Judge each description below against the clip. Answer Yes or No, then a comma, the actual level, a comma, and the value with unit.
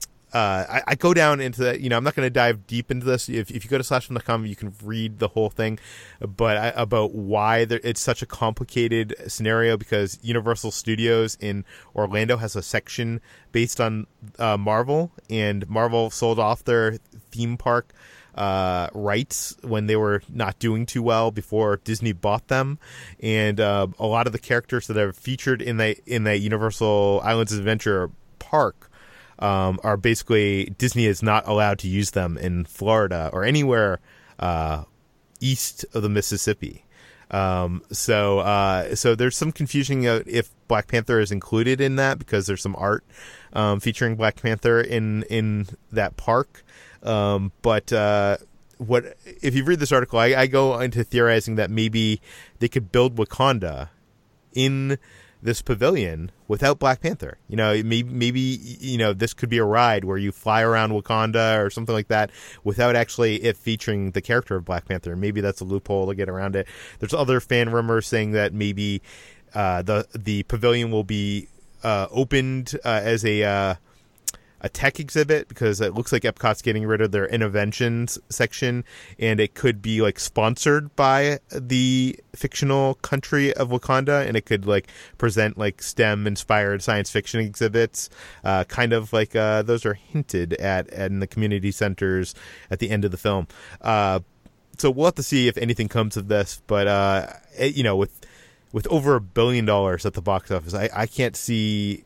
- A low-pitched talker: Yes, low, 110 Hz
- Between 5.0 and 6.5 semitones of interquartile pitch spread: No, average, 3.0 semitones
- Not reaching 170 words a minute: No, average, 180 wpm